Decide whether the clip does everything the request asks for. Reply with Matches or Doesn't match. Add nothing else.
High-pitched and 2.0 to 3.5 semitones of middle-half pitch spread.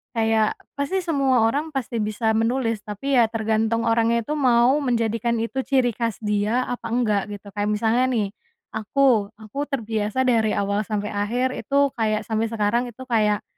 Matches